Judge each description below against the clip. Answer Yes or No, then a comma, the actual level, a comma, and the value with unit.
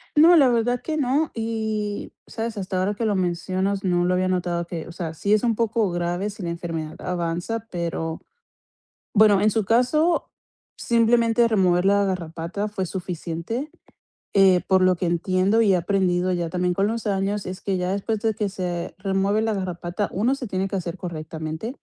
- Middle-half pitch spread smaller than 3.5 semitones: No, average, 3.8 semitones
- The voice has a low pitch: No, high, 195 Hz